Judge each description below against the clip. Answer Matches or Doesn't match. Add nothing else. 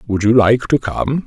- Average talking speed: Doesn't match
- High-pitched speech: Doesn't match